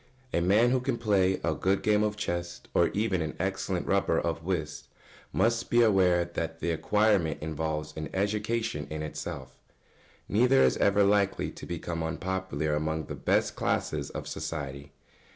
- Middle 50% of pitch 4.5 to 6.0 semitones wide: Yes, average, 4.9 semitones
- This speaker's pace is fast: No, average, 165 wpm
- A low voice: Yes, very low, 90 Hz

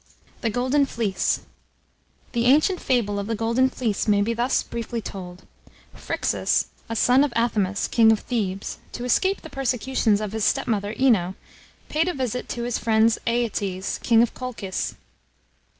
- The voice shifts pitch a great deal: No, average, 3.4 semitones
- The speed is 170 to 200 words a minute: No, average, 155 wpm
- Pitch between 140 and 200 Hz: No, high, 230 Hz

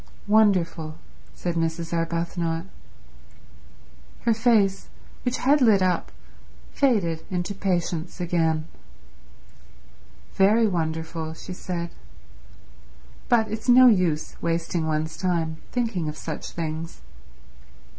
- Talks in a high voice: No, medium, 175 Hz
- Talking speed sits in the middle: No, slow, 95 wpm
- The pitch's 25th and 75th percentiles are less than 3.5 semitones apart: No, average, 4.1 semitones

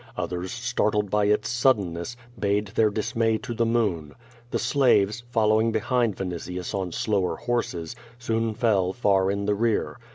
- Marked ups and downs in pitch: No, average, 3.2 semitones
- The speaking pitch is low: Yes, low, 105 Hz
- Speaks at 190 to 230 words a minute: No, average, 155 wpm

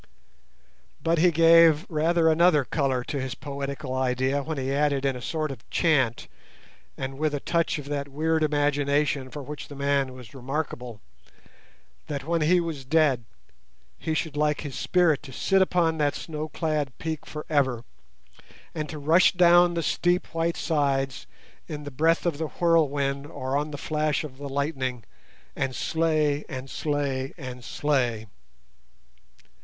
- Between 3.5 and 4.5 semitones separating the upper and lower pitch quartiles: No, average, 2.9 semitones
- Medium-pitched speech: Yes, medium, 145 Hz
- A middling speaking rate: Yes, average, 160 wpm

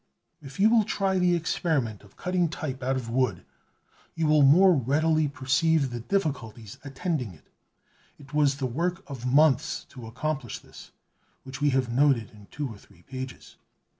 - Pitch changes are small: No, average, 4.1 semitones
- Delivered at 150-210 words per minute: Yes, average, 165 wpm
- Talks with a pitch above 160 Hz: No, medium, 140 Hz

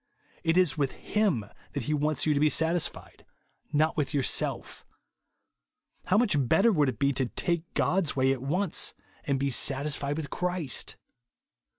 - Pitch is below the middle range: No, medium, 150 Hz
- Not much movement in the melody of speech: No, average, 3.7 semitones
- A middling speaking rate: Yes, average, 160 wpm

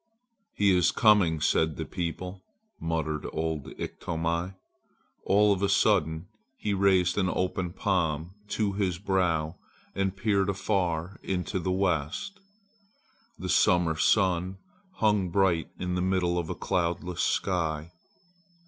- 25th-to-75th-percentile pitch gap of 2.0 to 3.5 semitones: Yes, average, 2.8 semitones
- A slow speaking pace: Yes, slow, 125 wpm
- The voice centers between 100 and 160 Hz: No, very low, 90 Hz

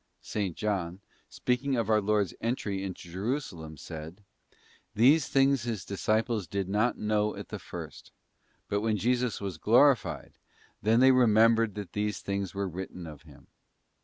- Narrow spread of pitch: No, average, 3.5 semitones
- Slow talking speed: No, average, 155 wpm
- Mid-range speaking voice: No, low, 105 Hz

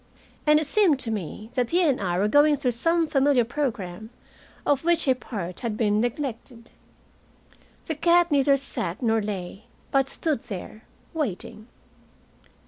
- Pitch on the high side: Yes, very high, 250 Hz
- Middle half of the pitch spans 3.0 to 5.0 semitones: No, wide, 5.5 semitones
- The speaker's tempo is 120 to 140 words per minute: No, average, 150 wpm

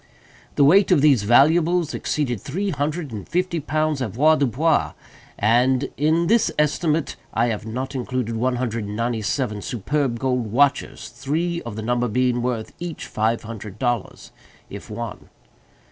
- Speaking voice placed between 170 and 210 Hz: No, low, 130 Hz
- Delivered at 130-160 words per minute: Yes, average, 150 wpm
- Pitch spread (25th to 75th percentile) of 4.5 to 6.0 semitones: Yes, average, 4.9 semitones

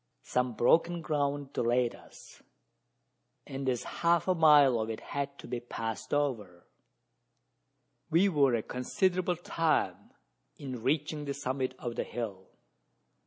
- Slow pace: Yes, slow, 130 wpm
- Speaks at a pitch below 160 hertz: Yes, low, 135 Hz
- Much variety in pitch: No, average, 4.3 semitones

